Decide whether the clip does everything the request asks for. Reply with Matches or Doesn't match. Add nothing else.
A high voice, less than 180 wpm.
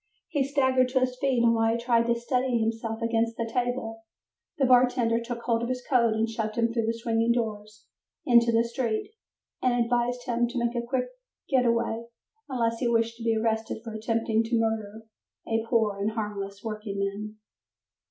Doesn't match